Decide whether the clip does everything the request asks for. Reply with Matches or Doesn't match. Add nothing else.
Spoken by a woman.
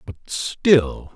Doesn't match